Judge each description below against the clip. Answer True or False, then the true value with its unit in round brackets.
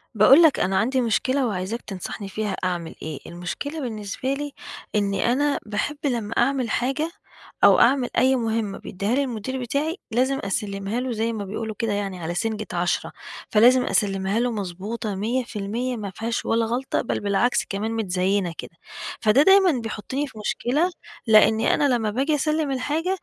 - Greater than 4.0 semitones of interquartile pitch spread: True (4.4 semitones)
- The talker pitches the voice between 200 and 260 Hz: True (225 Hz)